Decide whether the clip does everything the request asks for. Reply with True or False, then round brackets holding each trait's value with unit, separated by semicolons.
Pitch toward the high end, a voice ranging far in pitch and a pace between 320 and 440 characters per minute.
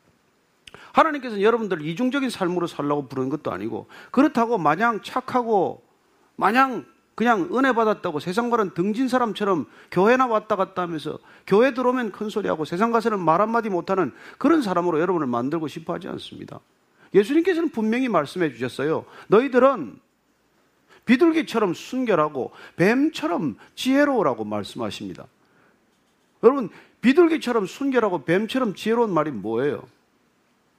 True (230 Hz; 6.3 semitones; 350 characters per minute)